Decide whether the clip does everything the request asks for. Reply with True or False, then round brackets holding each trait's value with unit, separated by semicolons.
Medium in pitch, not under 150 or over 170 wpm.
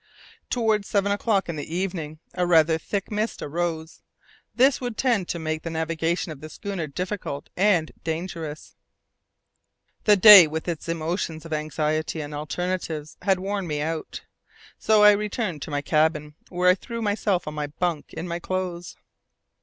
True (170 Hz; 160 wpm)